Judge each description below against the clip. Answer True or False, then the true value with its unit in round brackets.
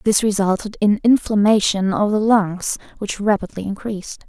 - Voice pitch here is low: False (205 Hz)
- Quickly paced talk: False (140 wpm)